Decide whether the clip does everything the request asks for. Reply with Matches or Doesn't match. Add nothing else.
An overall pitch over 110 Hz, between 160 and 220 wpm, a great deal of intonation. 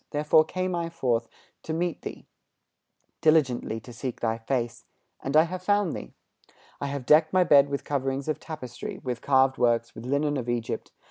Doesn't match